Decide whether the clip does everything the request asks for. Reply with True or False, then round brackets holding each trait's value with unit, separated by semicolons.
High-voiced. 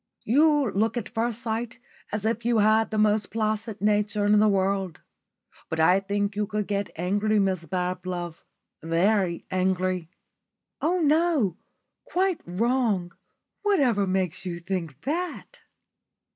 True (205 Hz)